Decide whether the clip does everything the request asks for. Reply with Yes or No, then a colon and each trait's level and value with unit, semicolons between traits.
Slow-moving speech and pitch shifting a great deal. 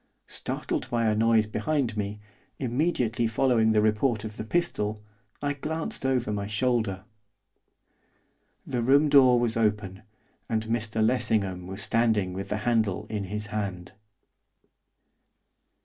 No: slow, 130 wpm; average, 2.7 semitones